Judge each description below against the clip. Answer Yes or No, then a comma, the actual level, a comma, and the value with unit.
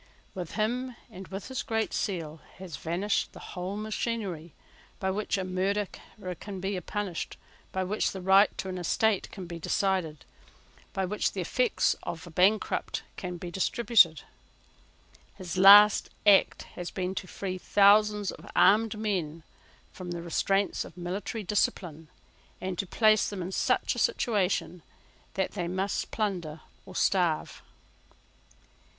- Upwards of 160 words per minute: No, average, 145 wpm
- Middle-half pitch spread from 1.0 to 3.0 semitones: Yes, average, 2.7 semitones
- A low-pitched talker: No, high, 190 Hz